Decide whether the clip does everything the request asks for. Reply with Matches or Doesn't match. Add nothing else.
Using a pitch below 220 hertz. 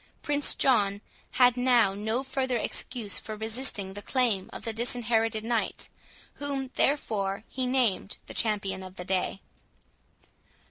Doesn't match